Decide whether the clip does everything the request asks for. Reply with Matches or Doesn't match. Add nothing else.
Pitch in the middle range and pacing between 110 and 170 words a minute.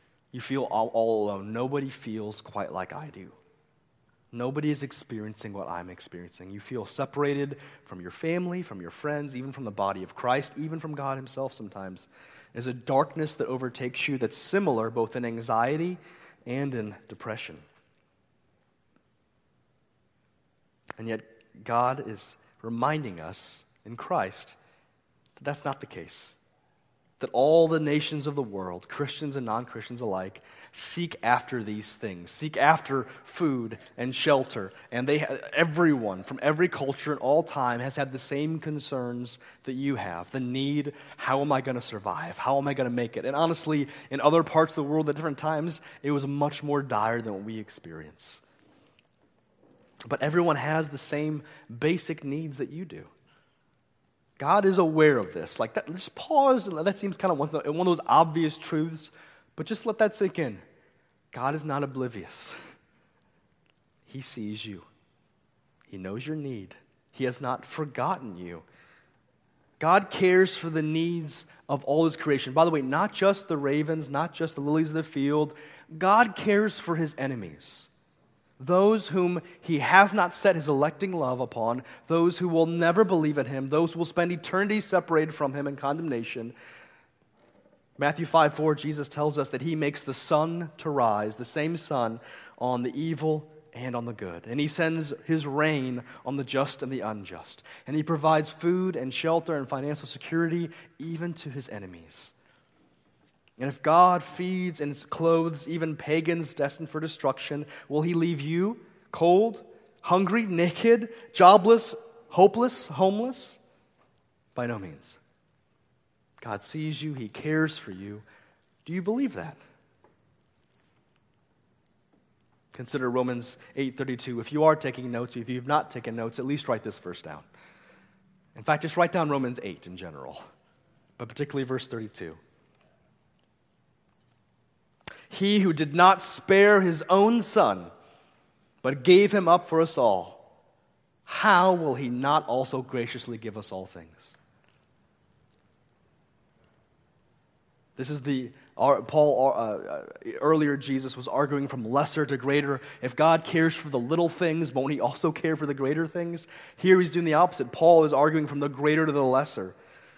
Matches